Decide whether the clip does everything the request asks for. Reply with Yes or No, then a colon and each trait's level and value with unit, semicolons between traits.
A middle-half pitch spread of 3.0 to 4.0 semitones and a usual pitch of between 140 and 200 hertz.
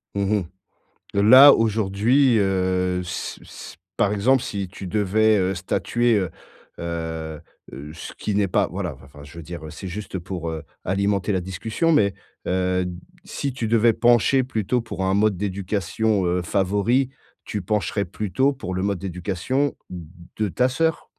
No: average, 3.6 semitones; low, 100 Hz